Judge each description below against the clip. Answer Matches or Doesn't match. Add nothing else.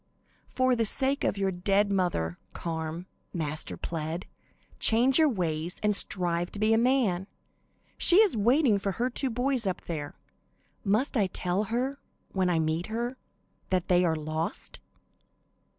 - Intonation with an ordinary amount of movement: Doesn't match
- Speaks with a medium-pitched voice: Doesn't match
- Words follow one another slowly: Doesn't match